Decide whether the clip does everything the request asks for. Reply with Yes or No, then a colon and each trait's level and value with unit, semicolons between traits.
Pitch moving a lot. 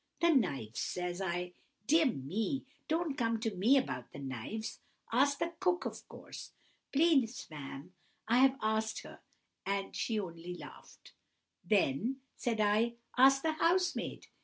Yes: wide, 7.3 semitones